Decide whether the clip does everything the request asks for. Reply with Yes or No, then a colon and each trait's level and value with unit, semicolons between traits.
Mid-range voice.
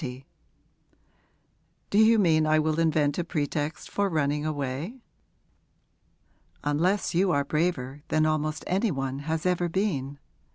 Yes: medium, 155 Hz